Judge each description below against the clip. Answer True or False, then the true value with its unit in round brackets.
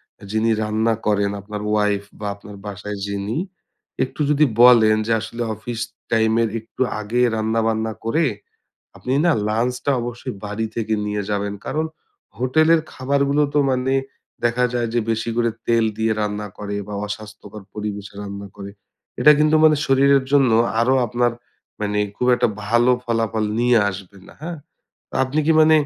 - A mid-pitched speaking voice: False (115 Hz)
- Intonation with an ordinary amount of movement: True (3.2 semitones)